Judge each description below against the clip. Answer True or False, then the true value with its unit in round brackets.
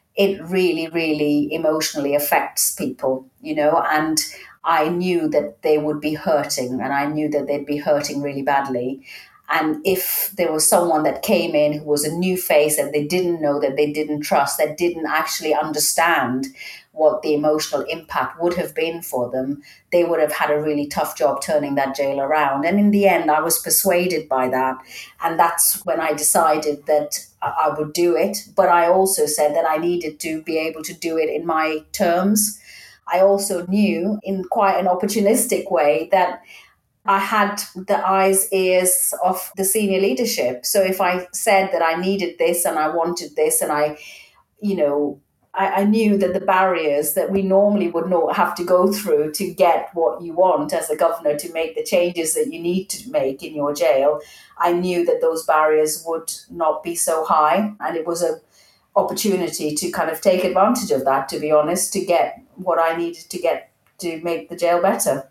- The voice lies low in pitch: False (165 Hz)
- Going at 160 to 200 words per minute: True (195 wpm)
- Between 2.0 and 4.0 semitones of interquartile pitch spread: True (3.7 semitones)